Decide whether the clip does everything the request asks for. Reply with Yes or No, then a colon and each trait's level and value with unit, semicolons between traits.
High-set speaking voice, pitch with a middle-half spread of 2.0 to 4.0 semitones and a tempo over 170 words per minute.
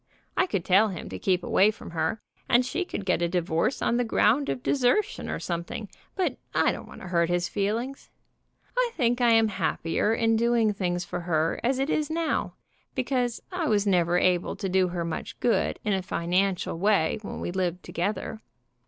No: high, 205 Hz; wide, 5.5 semitones; average, 195 wpm